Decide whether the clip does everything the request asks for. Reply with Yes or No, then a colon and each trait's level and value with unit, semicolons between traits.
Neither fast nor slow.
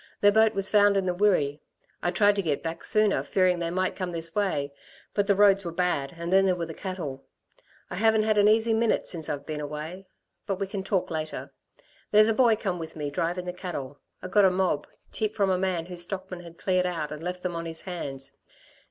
No: fast, 230 wpm